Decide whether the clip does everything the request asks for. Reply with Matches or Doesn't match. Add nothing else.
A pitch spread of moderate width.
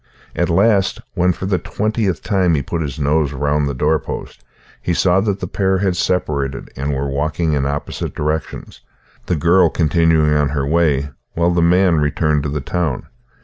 Matches